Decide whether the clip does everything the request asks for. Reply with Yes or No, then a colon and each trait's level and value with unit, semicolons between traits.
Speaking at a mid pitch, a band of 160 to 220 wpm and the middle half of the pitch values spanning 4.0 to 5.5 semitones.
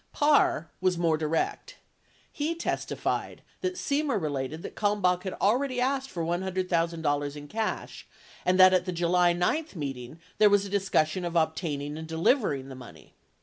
Yes: medium, 180 Hz; average, 165 wpm; average, 4.9 semitones